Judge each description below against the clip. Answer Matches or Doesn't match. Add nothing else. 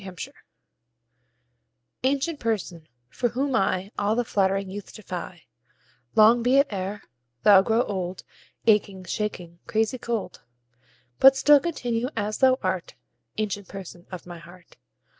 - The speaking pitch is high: Matches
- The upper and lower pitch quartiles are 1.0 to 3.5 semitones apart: Doesn't match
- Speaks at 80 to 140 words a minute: Matches